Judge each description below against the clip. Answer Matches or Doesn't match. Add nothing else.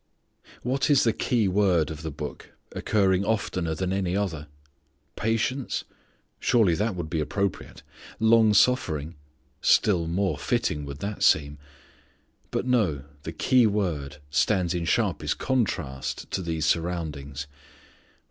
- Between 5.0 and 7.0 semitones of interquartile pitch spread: Matches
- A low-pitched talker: Matches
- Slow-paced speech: Matches